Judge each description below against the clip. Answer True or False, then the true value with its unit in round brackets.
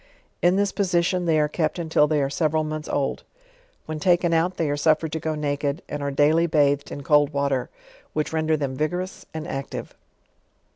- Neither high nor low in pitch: True (155 Hz)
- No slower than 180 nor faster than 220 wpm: True (190 wpm)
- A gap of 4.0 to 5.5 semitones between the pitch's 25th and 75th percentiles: False (2.4 semitones)